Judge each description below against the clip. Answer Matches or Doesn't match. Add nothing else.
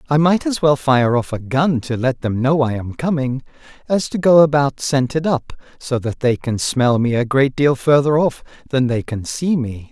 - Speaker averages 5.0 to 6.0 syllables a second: Doesn't match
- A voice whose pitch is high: Doesn't match